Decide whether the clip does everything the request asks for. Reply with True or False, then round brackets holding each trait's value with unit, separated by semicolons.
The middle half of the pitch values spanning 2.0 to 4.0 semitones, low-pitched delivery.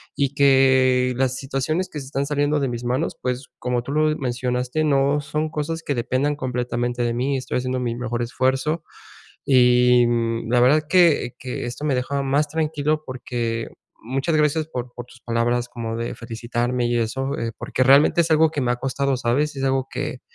True (2.9 semitones; 130 Hz)